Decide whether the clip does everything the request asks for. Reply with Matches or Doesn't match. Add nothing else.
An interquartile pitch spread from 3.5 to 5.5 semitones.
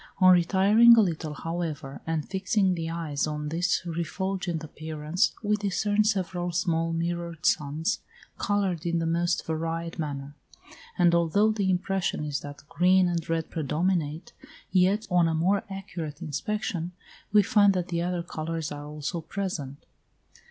Doesn't match